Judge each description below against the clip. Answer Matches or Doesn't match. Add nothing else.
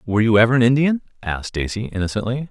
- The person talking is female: Doesn't match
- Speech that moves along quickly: Doesn't match